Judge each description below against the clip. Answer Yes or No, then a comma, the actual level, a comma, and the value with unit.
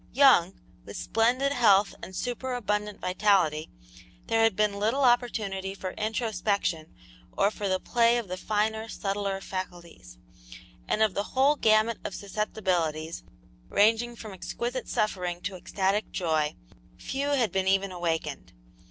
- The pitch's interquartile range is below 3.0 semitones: No, average, 3.5 semitones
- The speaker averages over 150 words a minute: No, slow, 135 wpm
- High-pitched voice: Yes, high, 205 Hz